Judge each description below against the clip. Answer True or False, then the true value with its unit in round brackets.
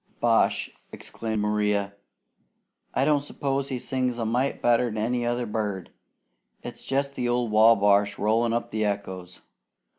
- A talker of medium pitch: False (115 Hz)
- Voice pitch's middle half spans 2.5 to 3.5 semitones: True (3.0 semitones)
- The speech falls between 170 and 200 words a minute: False (145 wpm)